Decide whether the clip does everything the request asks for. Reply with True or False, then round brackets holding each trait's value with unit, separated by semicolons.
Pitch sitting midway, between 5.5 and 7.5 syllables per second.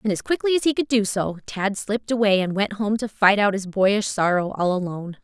False (205 Hz; 5.6 syllables/s)